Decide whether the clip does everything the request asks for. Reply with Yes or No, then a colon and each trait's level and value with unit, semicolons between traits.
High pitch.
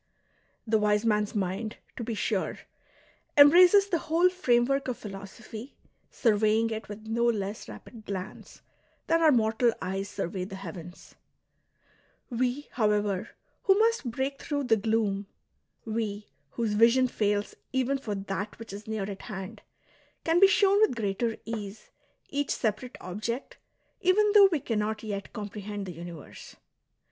Yes: high, 220 Hz